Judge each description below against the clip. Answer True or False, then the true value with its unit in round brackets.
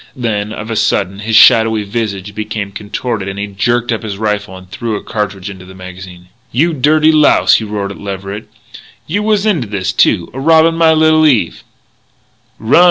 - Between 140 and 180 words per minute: False (190 wpm)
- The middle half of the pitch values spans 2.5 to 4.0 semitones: False (4.5 semitones)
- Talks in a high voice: False (105 Hz)